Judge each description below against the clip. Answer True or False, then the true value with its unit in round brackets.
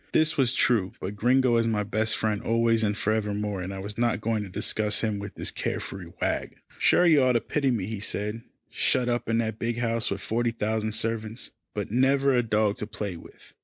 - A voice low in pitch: True (110 Hz)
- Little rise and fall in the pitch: True (2.2 semitones)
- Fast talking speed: True (220 wpm)